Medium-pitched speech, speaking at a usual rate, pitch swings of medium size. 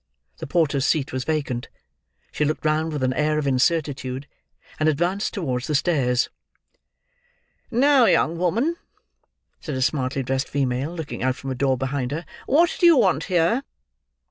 Yes: medium, 150 Hz; average, 160 wpm; average, 4.4 semitones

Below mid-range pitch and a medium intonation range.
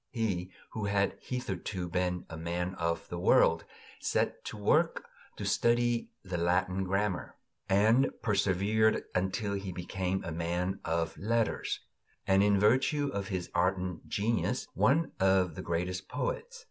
Yes: very low, 95 Hz; average, 3.4 semitones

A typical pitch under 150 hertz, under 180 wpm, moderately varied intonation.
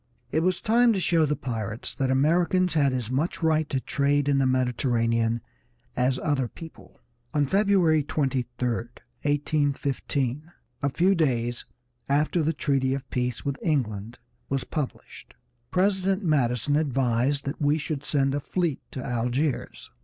Yes: medium, 140 Hz; average, 145 wpm; average, 3.8 semitones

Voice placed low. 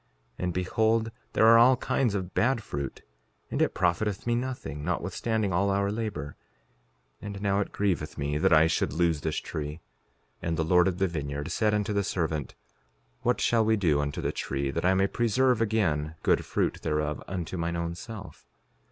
Yes: very low, 95 Hz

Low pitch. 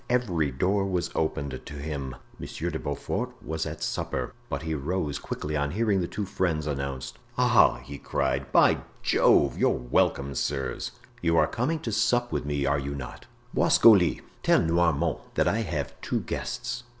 Yes: very low, 75 Hz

